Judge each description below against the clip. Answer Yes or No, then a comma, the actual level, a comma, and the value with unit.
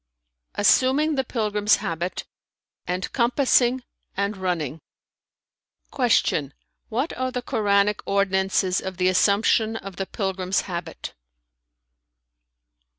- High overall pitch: Yes, high, 200 Hz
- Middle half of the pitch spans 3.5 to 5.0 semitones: Yes, average, 4.4 semitones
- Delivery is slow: Yes, slow, 95 wpm